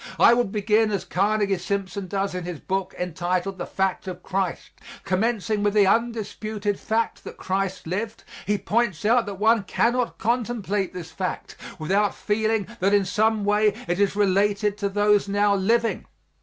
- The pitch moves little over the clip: Yes, narrow, 2.2 semitones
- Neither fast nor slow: Yes, average, 165 wpm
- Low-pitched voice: No, high, 205 Hz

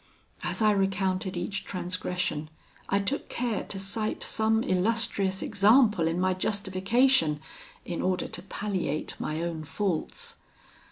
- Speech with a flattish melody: No, average, 3.0 semitones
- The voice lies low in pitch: No, high, 195 Hz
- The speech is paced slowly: Yes, slow, 125 wpm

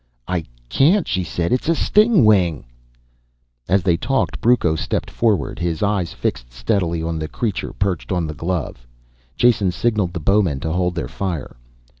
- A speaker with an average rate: Yes, average, 160 wpm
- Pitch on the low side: Yes, very low, 90 Hz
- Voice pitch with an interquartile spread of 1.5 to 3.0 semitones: No, average, 4.5 semitones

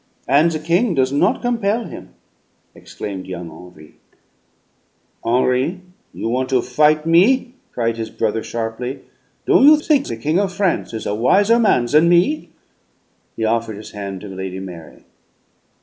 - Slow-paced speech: No, average, 150 wpm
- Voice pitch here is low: Yes, low, 130 Hz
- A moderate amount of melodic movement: No, wide, 8.8 semitones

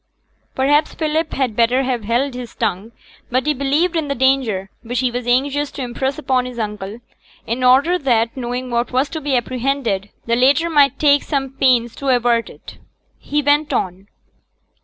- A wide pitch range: No, average, 3.0 semitones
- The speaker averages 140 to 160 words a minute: No, average, 180 wpm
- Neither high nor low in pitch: No, very high, 255 Hz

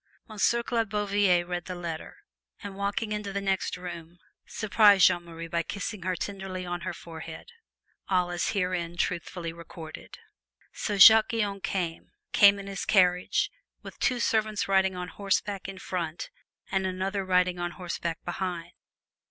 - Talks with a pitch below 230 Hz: Yes, medium, 185 Hz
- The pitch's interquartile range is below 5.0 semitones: Yes, narrow, 2.4 semitones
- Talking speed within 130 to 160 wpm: Yes, average, 150 wpm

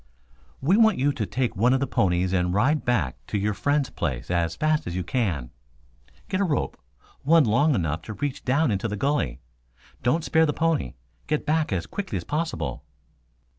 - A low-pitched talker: Yes, low, 125 Hz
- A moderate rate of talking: Yes, average, 190 wpm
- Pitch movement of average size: No, wide, 8.5 semitones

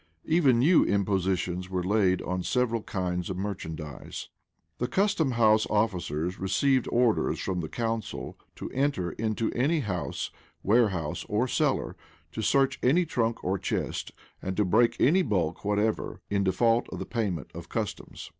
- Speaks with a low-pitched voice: Yes, low, 105 Hz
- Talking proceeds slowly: No, average, 150 wpm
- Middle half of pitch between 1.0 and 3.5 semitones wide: No, average, 4.8 semitones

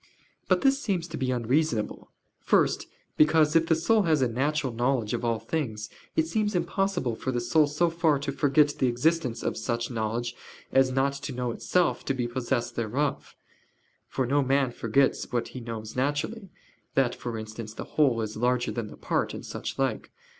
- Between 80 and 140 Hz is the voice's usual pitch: Yes, low, 135 Hz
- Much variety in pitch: No, average, 4.6 semitones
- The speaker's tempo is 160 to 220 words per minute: Yes, average, 185 wpm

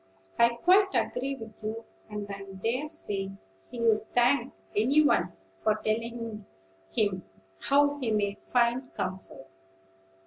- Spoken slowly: Yes, slow, 125 wpm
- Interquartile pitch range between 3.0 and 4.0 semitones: Yes, average, 3.6 semitones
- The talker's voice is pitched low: No, high, 230 Hz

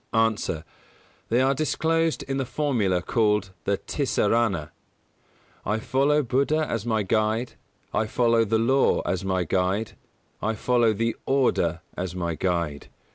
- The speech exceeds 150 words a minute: No, average, 140 wpm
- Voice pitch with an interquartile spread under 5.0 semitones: No, average, 5.3 semitones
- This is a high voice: No, low, 110 Hz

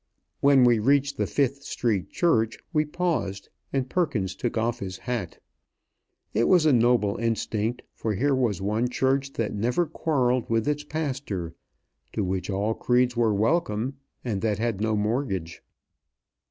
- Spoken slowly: No, average, 155 wpm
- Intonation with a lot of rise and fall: No, average, 4.7 semitones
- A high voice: No, low, 120 Hz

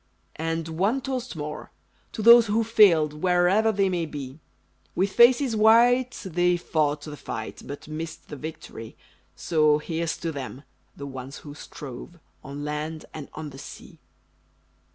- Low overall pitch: No, medium, 160 Hz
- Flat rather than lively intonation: No, wide, 5.6 semitones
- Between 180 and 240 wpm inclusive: No, average, 150 wpm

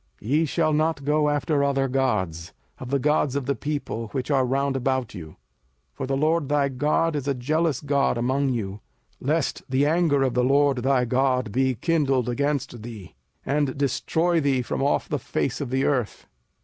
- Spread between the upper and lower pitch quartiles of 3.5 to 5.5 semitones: No, average, 2.7 semitones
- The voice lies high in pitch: No, low, 135 Hz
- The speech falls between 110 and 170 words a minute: No, average, 190 wpm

